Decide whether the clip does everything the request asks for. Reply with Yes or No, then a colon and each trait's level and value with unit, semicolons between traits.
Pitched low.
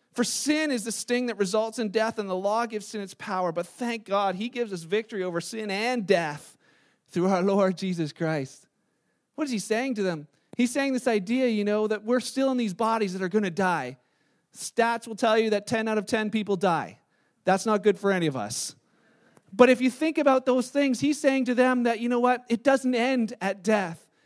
No: high, 220 Hz